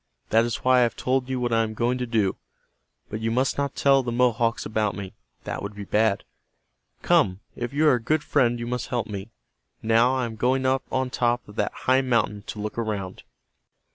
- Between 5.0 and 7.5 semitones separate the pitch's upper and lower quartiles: No, average, 2.7 semitones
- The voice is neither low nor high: No, low, 120 Hz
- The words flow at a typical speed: No, fast, 220 wpm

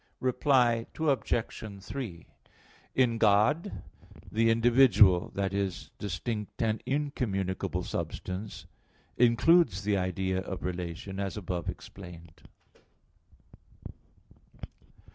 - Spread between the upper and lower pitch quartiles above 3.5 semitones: Yes, average, 4.2 semitones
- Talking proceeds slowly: Yes, slow, 80 wpm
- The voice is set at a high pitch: No, low, 105 Hz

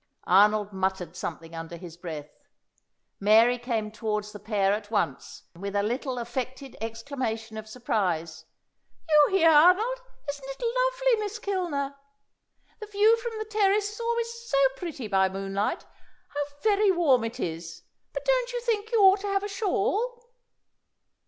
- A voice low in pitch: No, very high, 265 Hz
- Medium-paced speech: Yes, average, 150 wpm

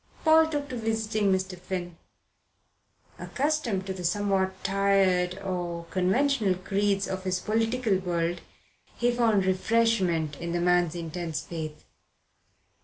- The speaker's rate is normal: No, slow, 120 wpm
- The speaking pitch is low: No, high, 190 Hz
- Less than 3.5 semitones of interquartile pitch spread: No, average, 3.8 semitones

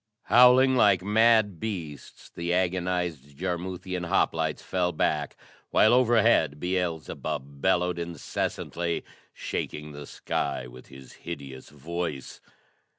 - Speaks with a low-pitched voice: Yes, very low, 90 Hz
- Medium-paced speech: No, slow, 100 wpm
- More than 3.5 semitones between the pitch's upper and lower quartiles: Yes, average, 3.9 semitones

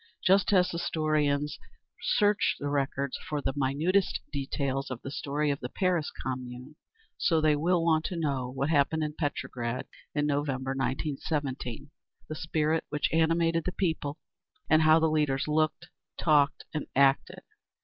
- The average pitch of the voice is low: No, medium, 150 Hz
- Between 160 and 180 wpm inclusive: No, average, 150 wpm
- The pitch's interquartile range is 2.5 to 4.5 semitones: Yes, average, 2.8 semitones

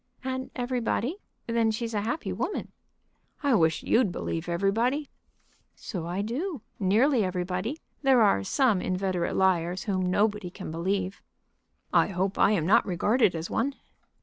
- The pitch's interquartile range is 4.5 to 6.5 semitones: Yes, average, 4.8 semitones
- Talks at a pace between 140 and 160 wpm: Yes, average, 145 wpm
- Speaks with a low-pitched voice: No, high, 200 Hz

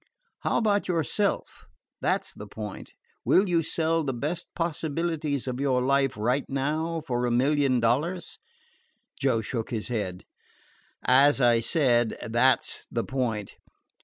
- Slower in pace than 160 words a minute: Yes, average, 140 wpm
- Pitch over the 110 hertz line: Yes, low, 135 Hz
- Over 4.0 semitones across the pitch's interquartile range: Yes, average, 5.1 semitones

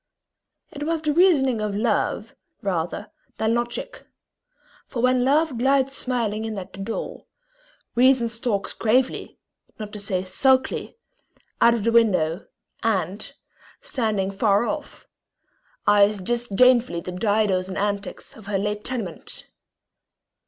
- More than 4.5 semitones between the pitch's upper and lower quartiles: No, average, 4.0 semitones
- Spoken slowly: Yes, slow, 125 wpm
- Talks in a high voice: Yes, high, 225 Hz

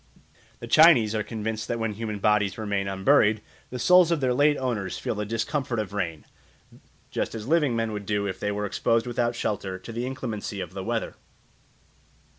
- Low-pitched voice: Yes, low, 110 Hz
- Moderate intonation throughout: Yes, average, 3.2 semitones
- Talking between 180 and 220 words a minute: Yes, average, 190 wpm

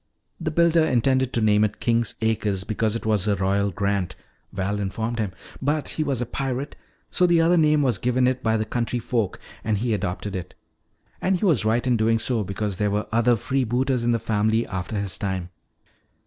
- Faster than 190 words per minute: Yes, fast, 205 wpm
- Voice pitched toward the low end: Yes, low, 115 Hz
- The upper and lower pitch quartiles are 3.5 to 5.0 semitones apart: Yes, average, 3.8 semitones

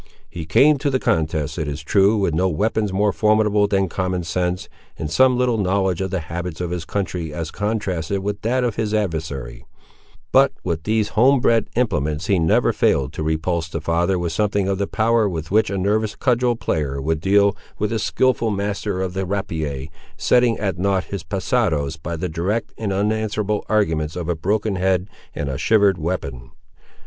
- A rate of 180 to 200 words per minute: Yes, average, 185 wpm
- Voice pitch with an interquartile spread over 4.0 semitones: Yes, average, 4.7 semitones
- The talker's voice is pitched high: No, very low, 95 Hz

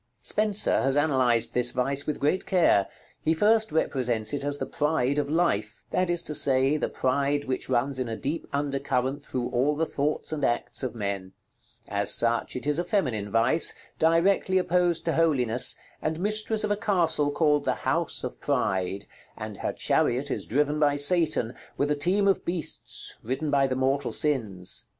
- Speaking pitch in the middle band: Yes, medium, 145 Hz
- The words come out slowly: No, average, 180 wpm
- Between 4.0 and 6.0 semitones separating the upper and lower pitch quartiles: Yes, average, 4.4 semitones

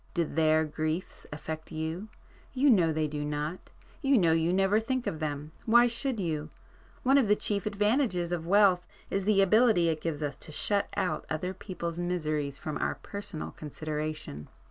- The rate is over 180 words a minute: No, average, 165 wpm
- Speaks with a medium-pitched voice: Yes, medium, 170 Hz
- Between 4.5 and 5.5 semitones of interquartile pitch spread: Yes, average, 4.8 semitones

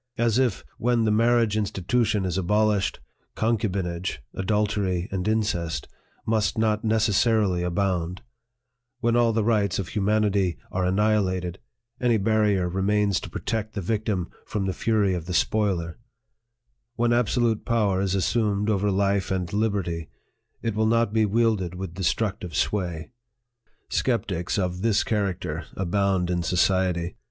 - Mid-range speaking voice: No, low, 100 Hz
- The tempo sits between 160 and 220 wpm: No, slow, 135 wpm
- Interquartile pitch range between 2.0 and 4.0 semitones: Yes, average, 3.0 semitones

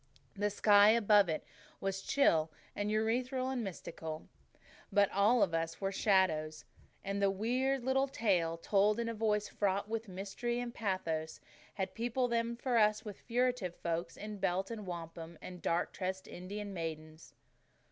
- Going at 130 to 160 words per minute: Yes, average, 155 wpm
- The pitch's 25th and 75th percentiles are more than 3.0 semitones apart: Yes, average, 4.4 semitones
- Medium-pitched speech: No, high, 200 Hz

